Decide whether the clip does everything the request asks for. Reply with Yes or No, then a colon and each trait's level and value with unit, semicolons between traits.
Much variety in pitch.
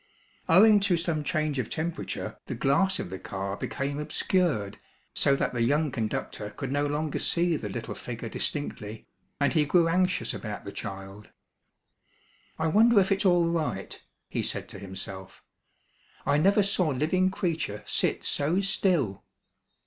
Yes: wide, 8.2 semitones